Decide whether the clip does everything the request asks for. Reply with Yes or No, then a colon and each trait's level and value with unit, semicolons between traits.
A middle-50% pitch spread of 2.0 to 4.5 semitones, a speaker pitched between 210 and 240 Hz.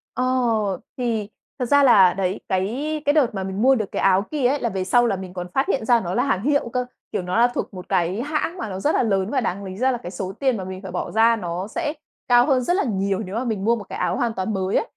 No: average, 5.0 semitones; high, 220 Hz